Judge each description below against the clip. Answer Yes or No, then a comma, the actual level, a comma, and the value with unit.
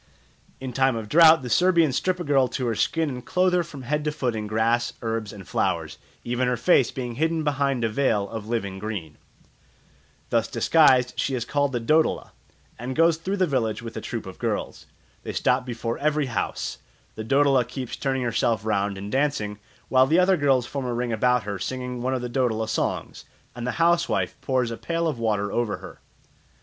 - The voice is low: Yes, low, 125 Hz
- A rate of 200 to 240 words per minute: Yes, fast, 205 wpm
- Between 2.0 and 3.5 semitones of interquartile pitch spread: No, average, 4.2 semitones